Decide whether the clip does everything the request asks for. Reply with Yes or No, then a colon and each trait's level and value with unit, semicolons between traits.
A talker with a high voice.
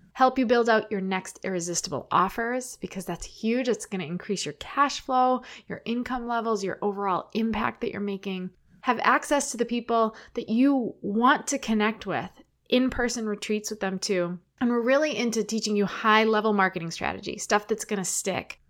Yes: high, 220 Hz